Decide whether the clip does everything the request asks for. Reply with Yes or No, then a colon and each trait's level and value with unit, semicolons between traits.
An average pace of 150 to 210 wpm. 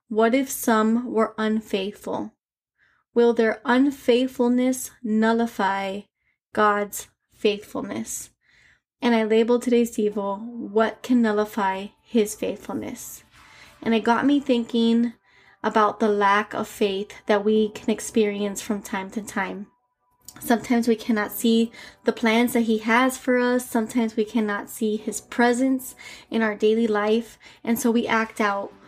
No: slow, 135 wpm